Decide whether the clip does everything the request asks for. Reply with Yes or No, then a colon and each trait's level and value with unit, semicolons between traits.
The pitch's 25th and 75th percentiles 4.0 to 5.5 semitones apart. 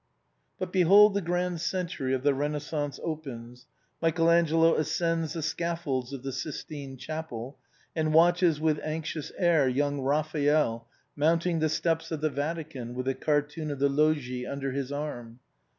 No: average, 3.2 semitones